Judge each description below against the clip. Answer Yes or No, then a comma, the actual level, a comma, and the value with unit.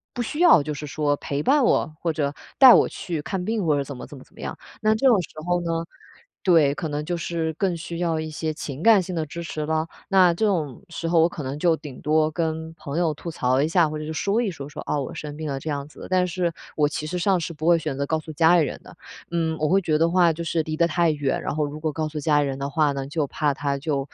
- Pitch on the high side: No, medium, 160 Hz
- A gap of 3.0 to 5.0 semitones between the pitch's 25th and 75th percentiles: No, narrow, 2.6 semitones